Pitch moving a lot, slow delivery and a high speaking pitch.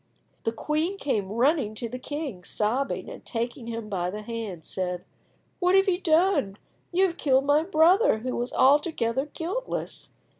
No: wide, 6.7 semitones; average, 160 wpm; very high, 260 Hz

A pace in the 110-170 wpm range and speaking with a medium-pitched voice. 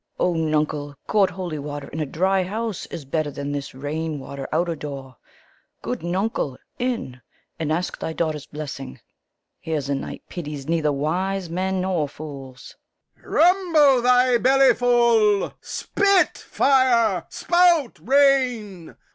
Yes: average, 140 wpm; medium, 175 Hz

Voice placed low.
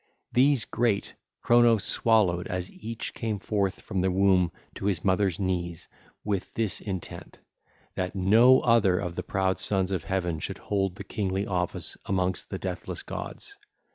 Yes: very low, 95 Hz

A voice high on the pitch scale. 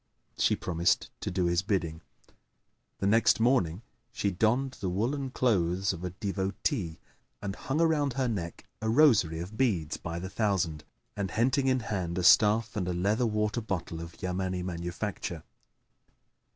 No: low, 100 Hz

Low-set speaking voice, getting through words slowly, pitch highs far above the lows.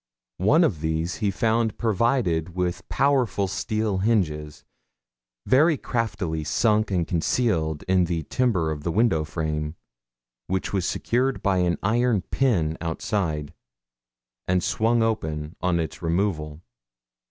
Yes: very low, 95 Hz; slow, 125 wpm; wide, 5.8 semitones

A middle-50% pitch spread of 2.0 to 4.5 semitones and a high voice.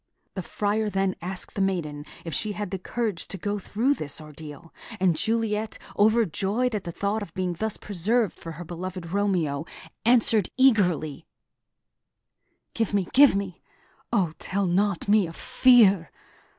Yes: average, 3.8 semitones; high, 195 Hz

